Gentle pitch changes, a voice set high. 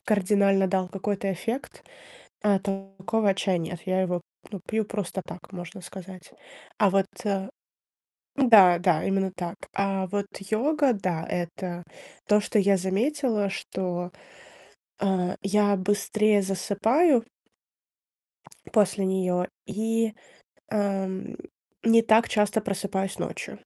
Yes: narrow, 2.2 semitones; high, 195 Hz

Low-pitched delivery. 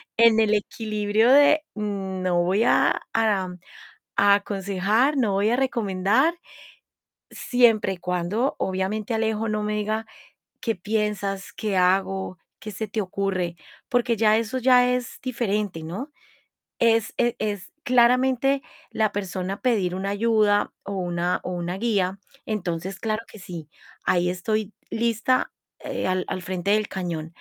No: high, 210 Hz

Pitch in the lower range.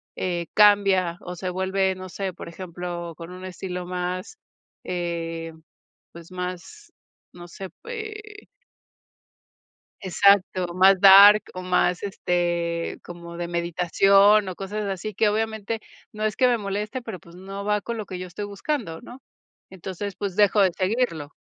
No: medium, 185 Hz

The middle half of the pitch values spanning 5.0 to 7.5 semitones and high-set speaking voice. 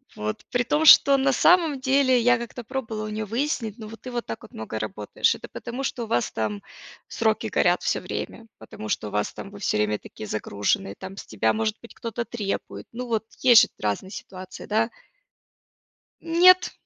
Yes: wide, 5.5 semitones; high, 225 Hz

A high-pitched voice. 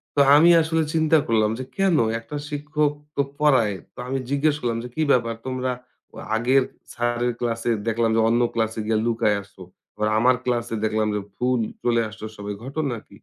No: low, 120 Hz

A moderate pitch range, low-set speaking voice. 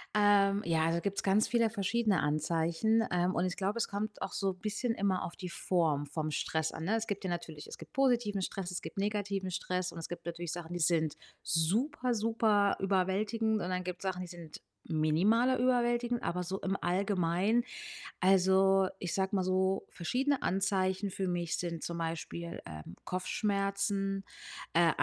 No: average, 3.2 semitones; high, 190 Hz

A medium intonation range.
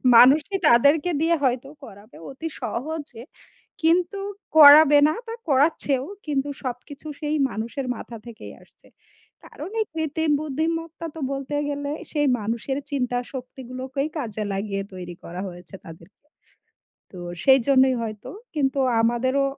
Yes: average, 4.4 semitones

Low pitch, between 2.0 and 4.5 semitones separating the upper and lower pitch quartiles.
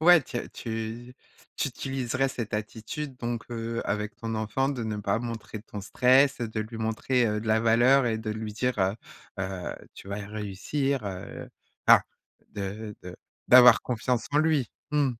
Yes: low, 115 Hz; average, 3.0 semitones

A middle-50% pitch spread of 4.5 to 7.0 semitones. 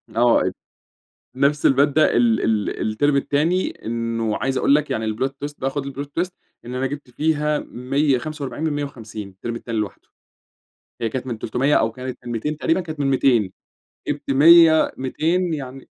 No: average, 3.9 semitones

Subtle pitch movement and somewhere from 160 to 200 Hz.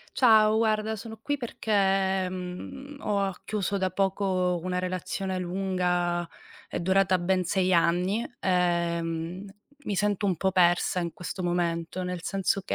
Yes: narrow, 2.0 semitones; medium, 185 Hz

